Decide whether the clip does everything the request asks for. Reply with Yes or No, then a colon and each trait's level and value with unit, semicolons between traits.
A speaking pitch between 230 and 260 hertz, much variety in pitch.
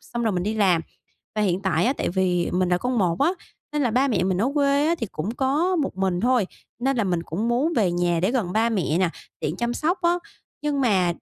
No: high, 220 Hz; wide, 6.5 semitones